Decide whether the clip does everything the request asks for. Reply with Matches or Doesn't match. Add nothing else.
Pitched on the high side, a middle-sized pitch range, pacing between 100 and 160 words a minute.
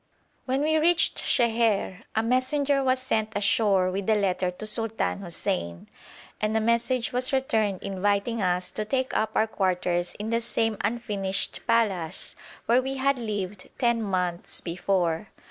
Matches